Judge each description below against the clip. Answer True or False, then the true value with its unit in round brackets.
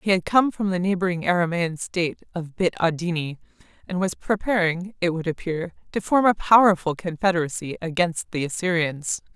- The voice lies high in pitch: False (175 Hz)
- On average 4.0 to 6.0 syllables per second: True (5.3 syllables/s)